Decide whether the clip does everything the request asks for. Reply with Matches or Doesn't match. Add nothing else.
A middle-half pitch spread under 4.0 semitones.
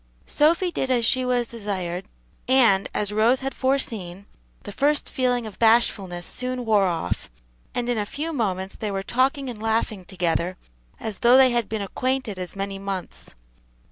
Doesn't match